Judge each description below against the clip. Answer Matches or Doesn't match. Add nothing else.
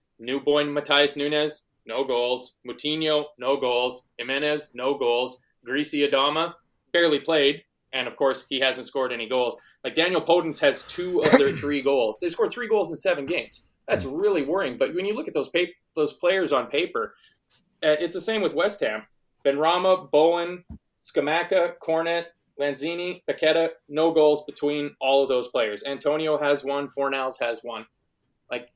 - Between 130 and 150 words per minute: Doesn't match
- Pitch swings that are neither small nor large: Matches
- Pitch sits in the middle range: Matches